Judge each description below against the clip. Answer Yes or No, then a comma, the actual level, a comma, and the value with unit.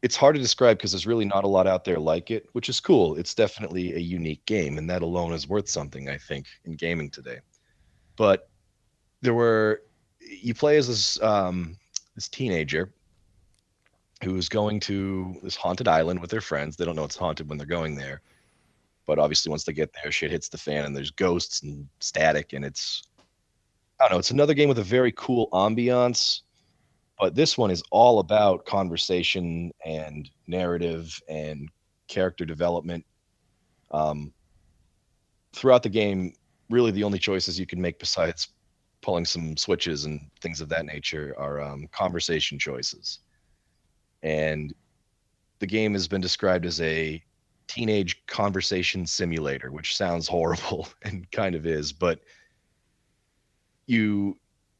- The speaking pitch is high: No, very low, 90 Hz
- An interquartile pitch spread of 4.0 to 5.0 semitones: Yes, average, 4.6 semitones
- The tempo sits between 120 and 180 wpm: Yes, average, 160 wpm